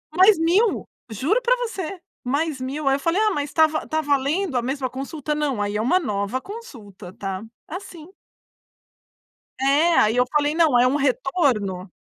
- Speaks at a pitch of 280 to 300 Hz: Yes, very high, 285 Hz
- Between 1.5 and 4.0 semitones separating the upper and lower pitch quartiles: No, average, 5.2 semitones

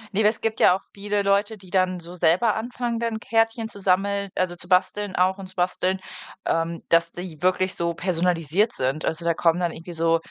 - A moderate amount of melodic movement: Yes, average, 3.1 semitones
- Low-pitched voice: No, medium, 185 Hz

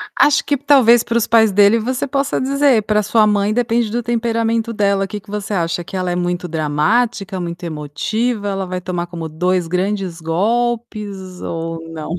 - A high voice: Yes, high, 205 Hz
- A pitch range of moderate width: Yes, average, 4.6 semitones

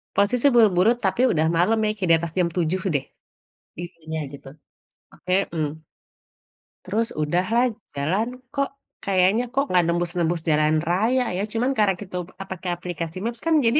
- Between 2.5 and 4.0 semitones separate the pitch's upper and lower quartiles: No, average, 4.8 semitones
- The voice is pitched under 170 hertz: No, medium, 185 Hz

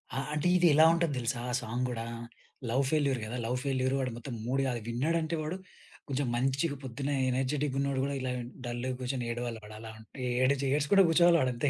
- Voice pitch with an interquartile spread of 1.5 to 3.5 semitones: Yes, average, 2.9 semitones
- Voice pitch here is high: No, low, 130 Hz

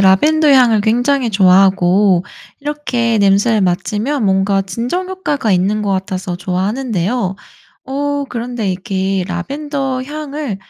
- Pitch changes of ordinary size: No, wide, 6.2 semitones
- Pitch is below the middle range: No, high, 215 Hz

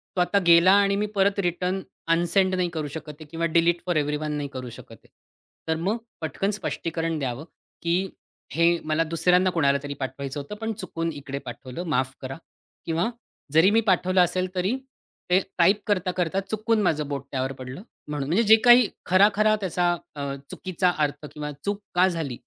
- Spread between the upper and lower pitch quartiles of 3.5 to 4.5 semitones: Yes, average, 4.1 semitones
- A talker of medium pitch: Yes, medium, 170 Hz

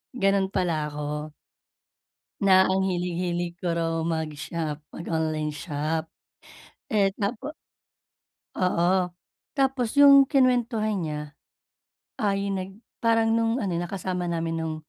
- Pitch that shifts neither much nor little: Yes, average, 4.5 semitones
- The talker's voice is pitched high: No, medium, 180 Hz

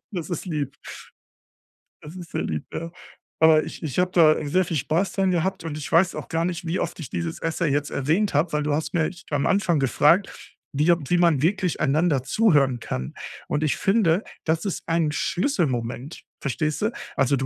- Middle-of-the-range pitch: Yes, medium, 160 Hz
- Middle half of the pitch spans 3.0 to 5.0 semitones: Yes, average, 3.6 semitones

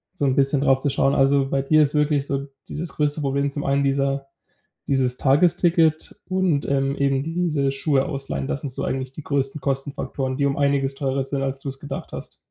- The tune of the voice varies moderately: No, narrow, 1.3 semitones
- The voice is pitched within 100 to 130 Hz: No, medium, 140 Hz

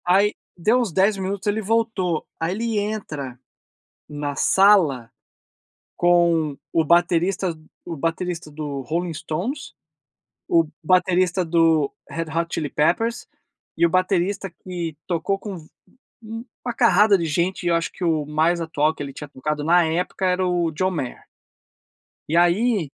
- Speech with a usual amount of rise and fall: Yes, average, 3.4 semitones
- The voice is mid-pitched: Yes, medium, 175 Hz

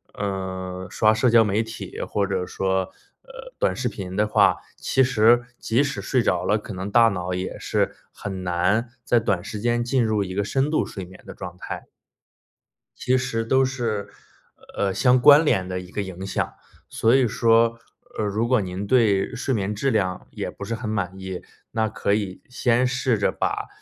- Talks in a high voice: No, low, 105 Hz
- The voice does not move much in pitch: No, average, 4.1 semitones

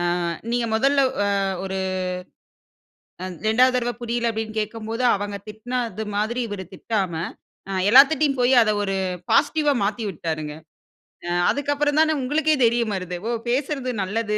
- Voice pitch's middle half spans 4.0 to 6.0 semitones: Yes, average, 4.3 semitones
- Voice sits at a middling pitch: No, high, 230 Hz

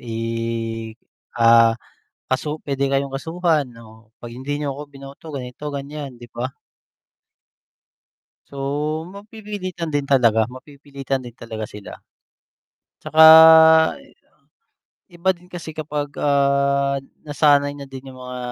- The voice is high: No, medium, 140 Hz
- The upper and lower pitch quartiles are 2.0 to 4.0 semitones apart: Yes, average, 2.9 semitones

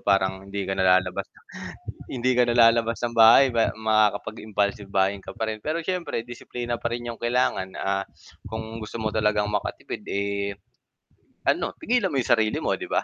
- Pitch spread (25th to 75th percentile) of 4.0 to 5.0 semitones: No, average, 2.9 semitones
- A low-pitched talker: Yes, low, 110 Hz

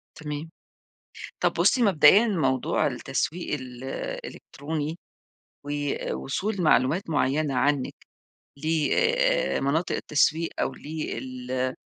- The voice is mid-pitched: Yes, medium, 150 Hz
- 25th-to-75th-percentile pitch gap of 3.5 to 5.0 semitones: Yes, average, 3.8 semitones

